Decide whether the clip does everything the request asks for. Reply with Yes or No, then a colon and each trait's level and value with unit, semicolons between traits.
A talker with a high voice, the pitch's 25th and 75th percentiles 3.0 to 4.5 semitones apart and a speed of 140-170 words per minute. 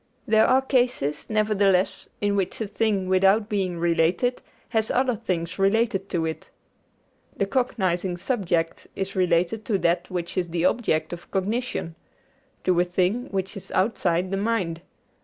Yes: high, 195 Hz; average, 3.7 semitones; average, 150 wpm